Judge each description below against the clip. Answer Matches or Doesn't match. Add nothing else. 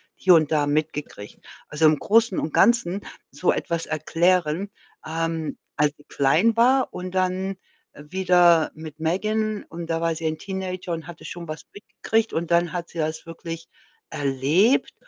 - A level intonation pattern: Doesn't match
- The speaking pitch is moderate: Matches